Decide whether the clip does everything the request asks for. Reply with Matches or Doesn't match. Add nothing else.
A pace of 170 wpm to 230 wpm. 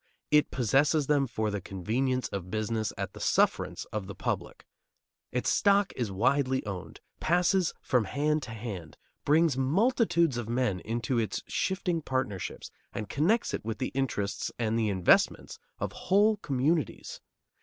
Doesn't match